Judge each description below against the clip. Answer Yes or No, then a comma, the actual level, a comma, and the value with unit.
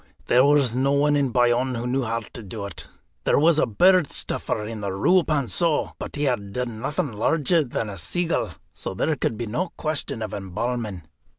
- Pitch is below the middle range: Yes, low, 125 Hz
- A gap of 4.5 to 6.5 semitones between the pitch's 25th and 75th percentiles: Yes, average, 5.2 semitones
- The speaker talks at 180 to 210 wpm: Yes, average, 200 wpm